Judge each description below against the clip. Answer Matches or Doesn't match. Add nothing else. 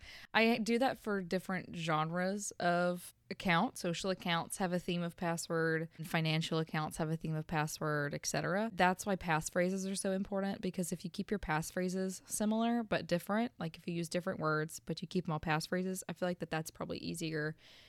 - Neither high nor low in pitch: Matches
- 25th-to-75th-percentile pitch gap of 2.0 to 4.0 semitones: Matches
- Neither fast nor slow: Matches